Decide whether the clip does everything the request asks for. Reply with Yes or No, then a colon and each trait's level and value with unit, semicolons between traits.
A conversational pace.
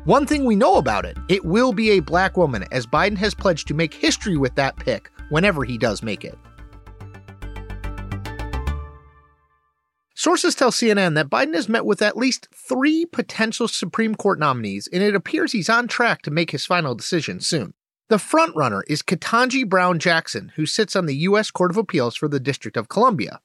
Yes: average, 185 wpm